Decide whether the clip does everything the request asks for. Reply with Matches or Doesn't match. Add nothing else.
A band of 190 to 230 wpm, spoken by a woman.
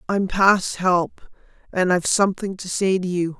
Doesn't match